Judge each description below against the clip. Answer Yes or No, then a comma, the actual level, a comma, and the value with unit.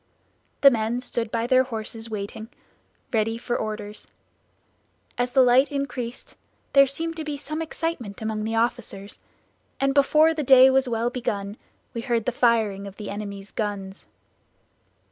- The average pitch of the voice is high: Yes, high, 235 Hz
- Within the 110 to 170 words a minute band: Yes, average, 150 wpm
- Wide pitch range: No, average, 3.7 semitones